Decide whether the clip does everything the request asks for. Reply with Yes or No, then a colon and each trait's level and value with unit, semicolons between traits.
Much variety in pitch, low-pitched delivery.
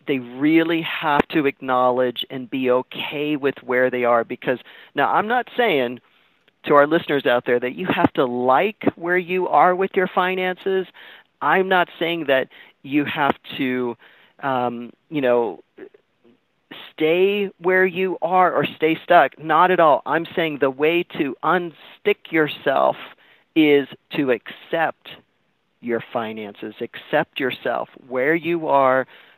No: wide, 6.0 semitones; medium, 150 Hz